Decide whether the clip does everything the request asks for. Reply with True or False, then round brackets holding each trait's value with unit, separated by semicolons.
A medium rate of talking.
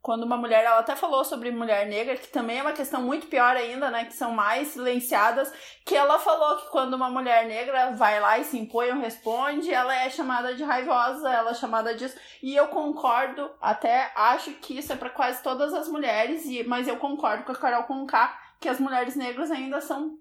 False (215 wpm)